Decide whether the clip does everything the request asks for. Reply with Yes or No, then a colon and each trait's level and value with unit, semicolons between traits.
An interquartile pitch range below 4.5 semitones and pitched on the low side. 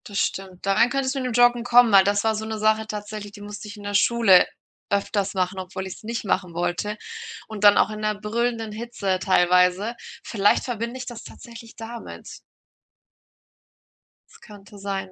No: average, 2.8 semitones; high, 210 Hz